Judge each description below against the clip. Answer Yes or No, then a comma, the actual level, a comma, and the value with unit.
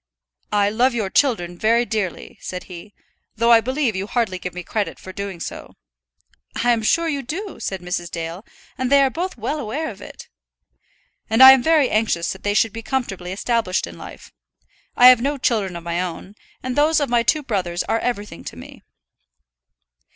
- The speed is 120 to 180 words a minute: No, average, 195 wpm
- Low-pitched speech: No, high, 225 Hz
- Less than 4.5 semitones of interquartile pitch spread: No, wide, 5.5 semitones